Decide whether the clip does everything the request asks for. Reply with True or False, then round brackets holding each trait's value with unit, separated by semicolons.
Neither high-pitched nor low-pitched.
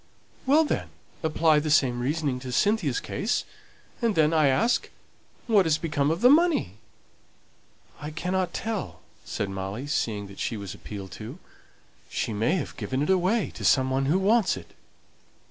True (150 Hz)